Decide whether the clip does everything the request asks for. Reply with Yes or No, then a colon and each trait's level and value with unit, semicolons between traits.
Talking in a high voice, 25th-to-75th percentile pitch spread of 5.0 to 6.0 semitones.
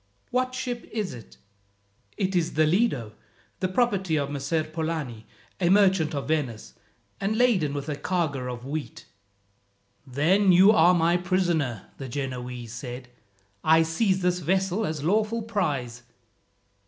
No: medium, 165 Hz; wide, 5.5 semitones